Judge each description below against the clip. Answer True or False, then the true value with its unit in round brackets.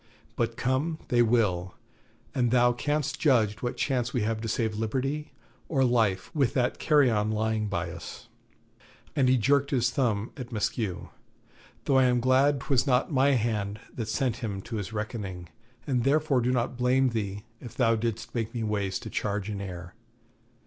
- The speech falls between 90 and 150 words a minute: False (175 wpm)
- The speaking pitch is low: True (120 Hz)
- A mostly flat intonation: False (3.5 semitones)